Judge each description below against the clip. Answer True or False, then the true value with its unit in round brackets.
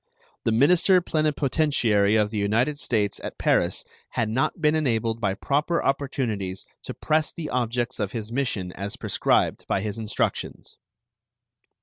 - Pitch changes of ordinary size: False (5.7 semitones)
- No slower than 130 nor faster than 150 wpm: True (140 wpm)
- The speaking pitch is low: True (115 Hz)